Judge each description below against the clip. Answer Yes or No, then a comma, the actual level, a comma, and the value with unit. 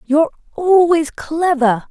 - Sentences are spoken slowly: Yes, slow, 95 wpm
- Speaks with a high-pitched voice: Yes, very high, 315 Hz